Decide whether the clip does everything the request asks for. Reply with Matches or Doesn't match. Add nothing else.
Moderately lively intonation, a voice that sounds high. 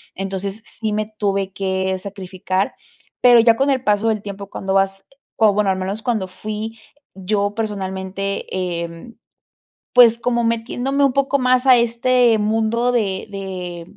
Matches